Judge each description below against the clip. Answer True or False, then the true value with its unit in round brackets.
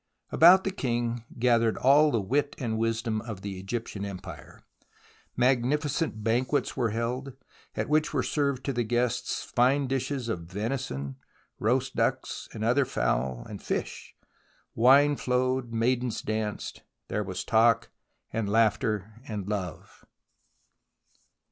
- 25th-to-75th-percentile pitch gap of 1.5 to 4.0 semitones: True (3.3 semitones)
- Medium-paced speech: False (130 wpm)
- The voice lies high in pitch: False (120 Hz)